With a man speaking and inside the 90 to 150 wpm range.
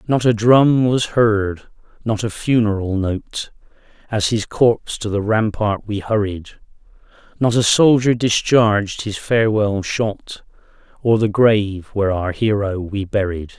Yes: male; average, 140 wpm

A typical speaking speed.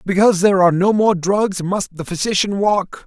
Yes: average, 195 wpm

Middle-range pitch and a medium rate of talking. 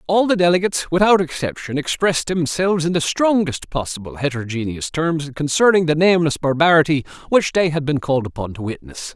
Yes: medium, 155 Hz; average, 165 wpm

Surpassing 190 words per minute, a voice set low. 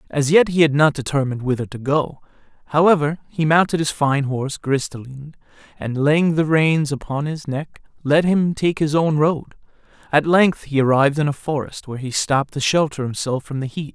No: average, 200 wpm; medium, 145 Hz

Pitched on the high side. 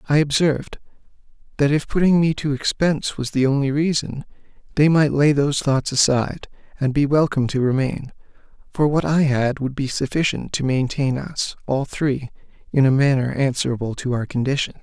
No: medium, 140 Hz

